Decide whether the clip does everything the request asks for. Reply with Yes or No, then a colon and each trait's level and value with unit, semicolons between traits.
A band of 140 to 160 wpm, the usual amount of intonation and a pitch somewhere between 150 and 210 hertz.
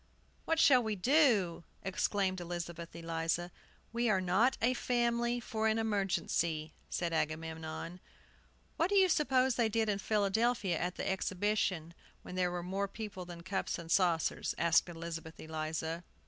Yes: average, 150 wpm; average, 4.9 semitones; medium, 185 Hz